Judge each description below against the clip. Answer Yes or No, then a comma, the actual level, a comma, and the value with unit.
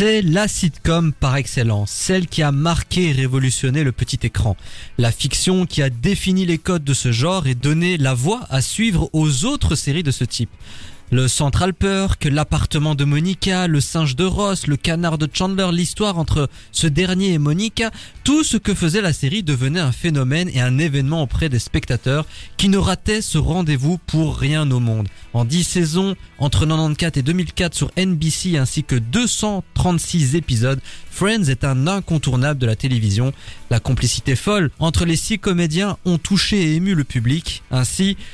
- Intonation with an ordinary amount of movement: No, wide, 5.7 semitones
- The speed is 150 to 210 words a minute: Yes, average, 180 wpm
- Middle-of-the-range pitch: Yes, medium, 150 Hz